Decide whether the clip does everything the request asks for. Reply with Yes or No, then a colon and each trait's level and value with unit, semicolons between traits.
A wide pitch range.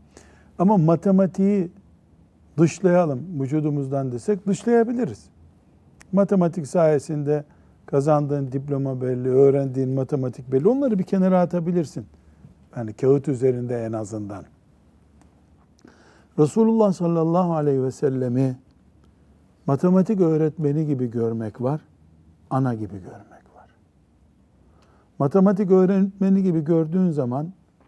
Yes: wide, 6.9 semitones